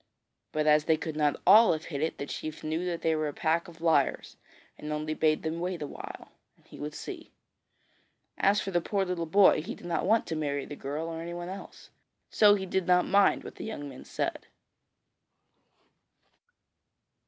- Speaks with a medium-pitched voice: Yes, medium, 165 Hz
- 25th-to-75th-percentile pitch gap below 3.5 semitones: Yes, average, 3.1 semitones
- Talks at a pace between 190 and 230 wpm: Yes, average, 200 wpm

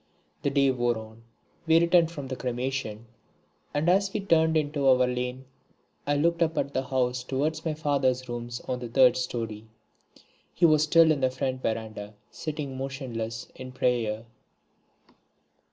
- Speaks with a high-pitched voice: No, low, 130 Hz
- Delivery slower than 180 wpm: Yes, average, 155 wpm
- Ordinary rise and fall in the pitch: Yes, average, 3.9 semitones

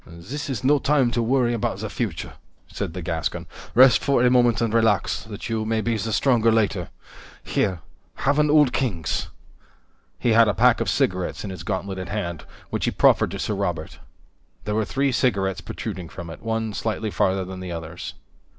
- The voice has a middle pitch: No, low, 110 Hz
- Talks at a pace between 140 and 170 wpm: No, average, 190 wpm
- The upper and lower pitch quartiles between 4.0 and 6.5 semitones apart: Yes, average, 4.4 semitones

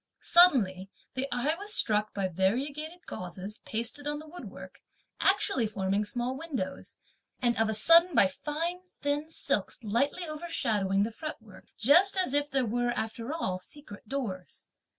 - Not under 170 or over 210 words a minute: No, average, 150 wpm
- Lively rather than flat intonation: Yes, wide, 6.6 semitones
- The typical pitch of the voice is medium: No, very high, 250 Hz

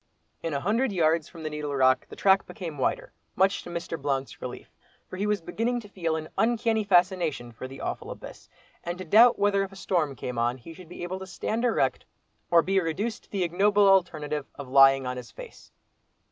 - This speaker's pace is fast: Yes, fast, 215 wpm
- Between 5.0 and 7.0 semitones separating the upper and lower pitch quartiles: Yes, average, 5.3 semitones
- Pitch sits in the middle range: Yes, medium, 175 Hz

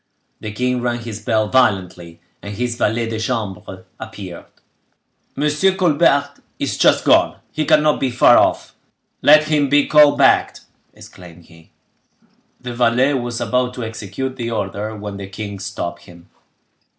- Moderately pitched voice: No, low, 115 Hz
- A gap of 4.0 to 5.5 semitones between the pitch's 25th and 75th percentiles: Yes, average, 4.7 semitones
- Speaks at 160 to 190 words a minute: No, average, 150 wpm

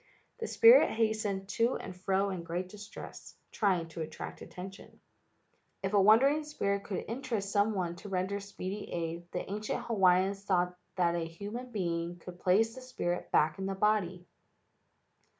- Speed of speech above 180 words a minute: No, average, 160 wpm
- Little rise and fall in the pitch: No, average, 3.1 semitones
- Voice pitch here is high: Yes, high, 195 Hz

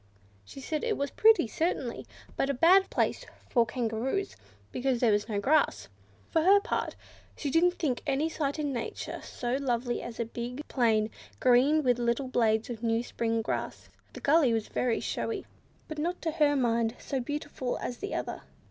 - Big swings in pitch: No, average, 4.6 semitones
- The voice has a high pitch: Yes, very high, 255 Hz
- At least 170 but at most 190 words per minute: Yes, average, 185 wpm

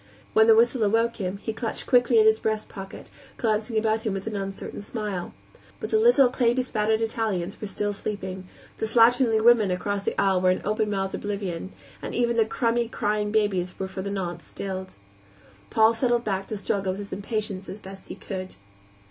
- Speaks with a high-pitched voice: Yes, high, 210 Hz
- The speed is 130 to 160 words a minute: No, average, 195 wpm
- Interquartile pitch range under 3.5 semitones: Yes, narrow, 2.6 semitones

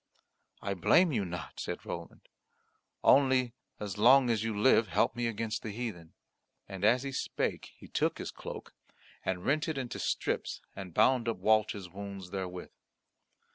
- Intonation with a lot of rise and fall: No, average, 4.4 semitones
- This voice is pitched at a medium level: No, low, 110 Hz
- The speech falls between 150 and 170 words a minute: Yes, average, 160 wpm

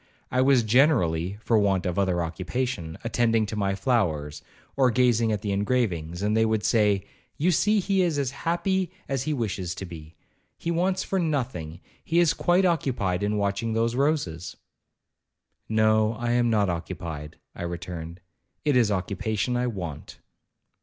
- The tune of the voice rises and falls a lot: Yes, wide, 6.1 semitones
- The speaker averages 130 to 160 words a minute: Yes, average, 155 wpm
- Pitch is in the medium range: No, low, 110 Hz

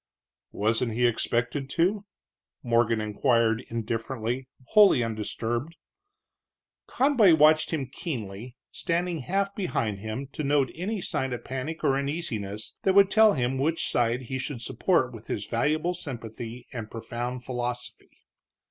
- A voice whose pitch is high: No, low, 130 Hz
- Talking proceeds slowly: Yes, slow, 130 wpm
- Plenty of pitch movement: Yes, wide, 5.8 semitones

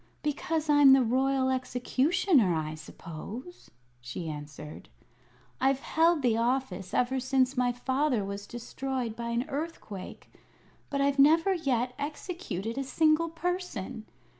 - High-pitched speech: Yes, very high, 260 Hz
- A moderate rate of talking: No, slow, 125 wpm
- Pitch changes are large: No, average, 4.7 semitones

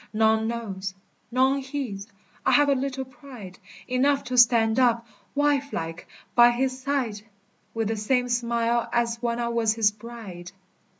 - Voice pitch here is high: Yes, high, 235 Hz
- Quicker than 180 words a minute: No, average, 145 wpm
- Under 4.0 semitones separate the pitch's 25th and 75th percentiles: Yes, average, 2.8 semitones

